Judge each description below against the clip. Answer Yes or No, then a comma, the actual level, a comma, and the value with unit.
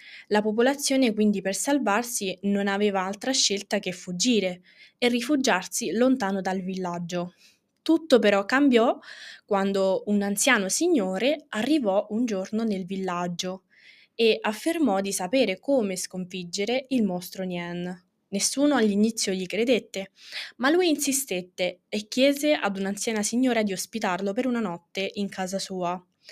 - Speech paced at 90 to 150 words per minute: Yes, average, 130 wpm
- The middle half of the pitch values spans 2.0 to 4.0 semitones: No, average, 4.7 semitones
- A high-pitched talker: Yes, high, 200 Hz